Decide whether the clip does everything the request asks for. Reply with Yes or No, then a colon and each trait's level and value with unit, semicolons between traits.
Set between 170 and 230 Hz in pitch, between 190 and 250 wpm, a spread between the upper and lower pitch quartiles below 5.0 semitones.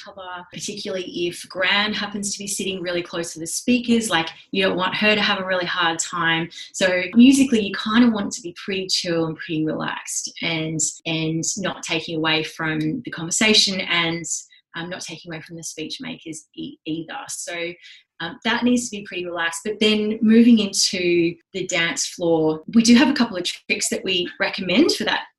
Yes: medium, 185 Hz; average, 200 wpm; average, 4.4 semitones